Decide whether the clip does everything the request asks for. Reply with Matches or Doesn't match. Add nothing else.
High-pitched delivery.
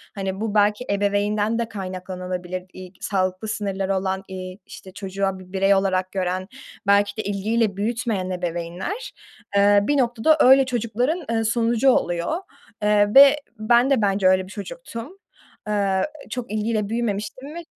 Matches